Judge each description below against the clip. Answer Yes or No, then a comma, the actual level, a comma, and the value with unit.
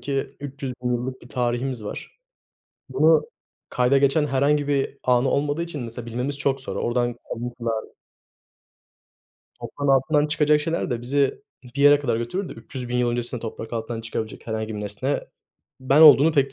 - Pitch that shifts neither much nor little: Yes, average, 3.0 semitones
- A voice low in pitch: Yes, low, 130 Hz